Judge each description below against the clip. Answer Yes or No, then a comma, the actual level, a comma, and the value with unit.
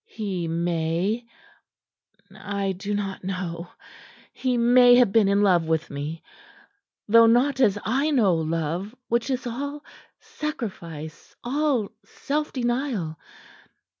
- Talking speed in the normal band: No, slow, 115 wpm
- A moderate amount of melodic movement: No, wide, 6.2 semitones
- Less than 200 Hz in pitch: No, high, 205 Hz